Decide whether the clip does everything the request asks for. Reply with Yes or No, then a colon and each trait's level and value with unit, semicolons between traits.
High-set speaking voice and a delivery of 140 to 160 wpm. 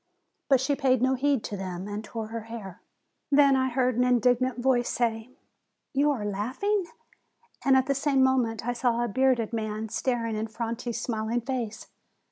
No: high, 240 Hz; average, 185 wpm